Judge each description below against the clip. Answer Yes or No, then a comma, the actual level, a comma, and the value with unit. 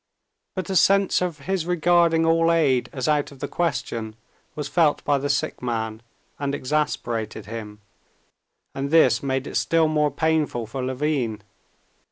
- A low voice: No, medium, 145 Hz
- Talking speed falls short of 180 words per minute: Yes, average, 155 wpm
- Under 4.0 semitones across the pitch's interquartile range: No, average, 4.5 semitones